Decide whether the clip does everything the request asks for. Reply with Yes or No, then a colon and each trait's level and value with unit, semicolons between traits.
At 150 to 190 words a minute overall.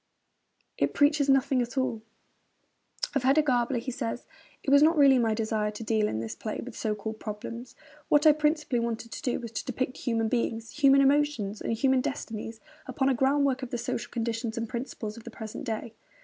No: average, 200 wpm